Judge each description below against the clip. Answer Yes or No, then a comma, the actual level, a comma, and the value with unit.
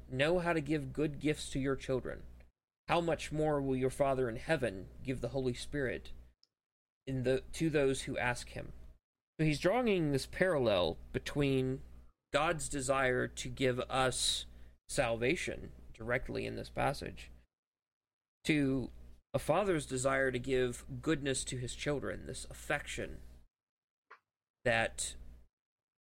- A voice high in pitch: No, low, 130 Hz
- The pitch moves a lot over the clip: Yes, wide, 7.0 semitones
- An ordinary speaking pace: No, slow, 130 wpm